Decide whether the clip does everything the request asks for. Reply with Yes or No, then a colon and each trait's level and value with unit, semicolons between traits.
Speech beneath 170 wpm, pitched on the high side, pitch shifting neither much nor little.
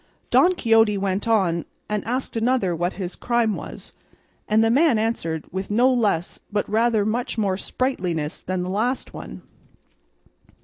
Yes: average, 150 wpm; high, 215 Hz; average, 4.1 semitones